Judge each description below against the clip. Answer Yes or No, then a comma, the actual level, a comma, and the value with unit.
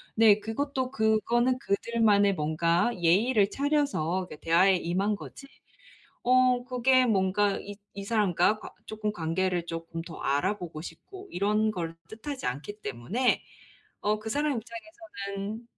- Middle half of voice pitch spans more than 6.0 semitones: No, average, 5.1 semitones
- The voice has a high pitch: Yes, high, 210 Hz